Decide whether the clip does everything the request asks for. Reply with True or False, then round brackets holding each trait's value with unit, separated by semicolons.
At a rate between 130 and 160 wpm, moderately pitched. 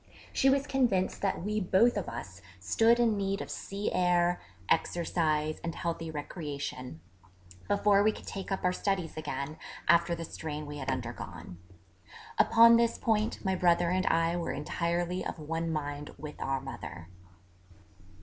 True (155 wpm; 170 Hz)